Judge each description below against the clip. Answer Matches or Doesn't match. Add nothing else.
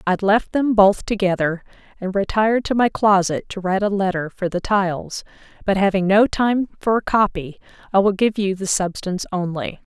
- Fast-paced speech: Doesn't match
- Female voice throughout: Matches